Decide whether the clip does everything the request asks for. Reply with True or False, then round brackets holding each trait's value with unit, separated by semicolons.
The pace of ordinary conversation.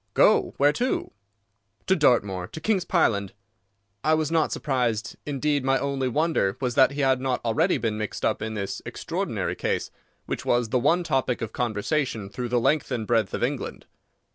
True (180 wpm)